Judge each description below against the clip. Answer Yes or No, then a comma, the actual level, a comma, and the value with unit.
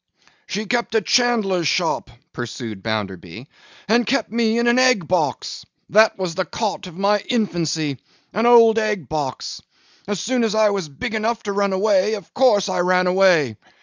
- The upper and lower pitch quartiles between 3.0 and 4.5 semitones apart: No, average, 5.2 semitones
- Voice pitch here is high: Yes, high, 200 Hz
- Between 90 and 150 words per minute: No, average, 175 wpm